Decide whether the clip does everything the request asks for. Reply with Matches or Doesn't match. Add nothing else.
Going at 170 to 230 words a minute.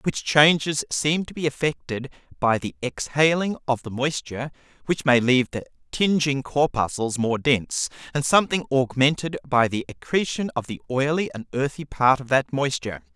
Doesn't match